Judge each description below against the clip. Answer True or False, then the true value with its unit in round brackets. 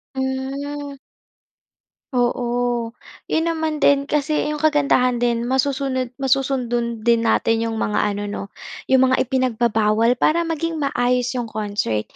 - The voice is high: True (255 Hz)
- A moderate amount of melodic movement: True (3.2 semitones)